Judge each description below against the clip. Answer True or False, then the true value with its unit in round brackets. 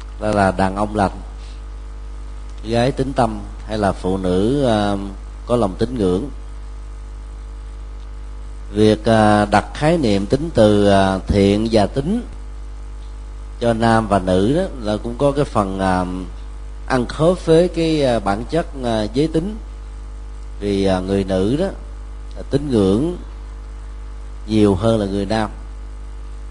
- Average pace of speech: False (140 wpm)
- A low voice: True (100 Hz)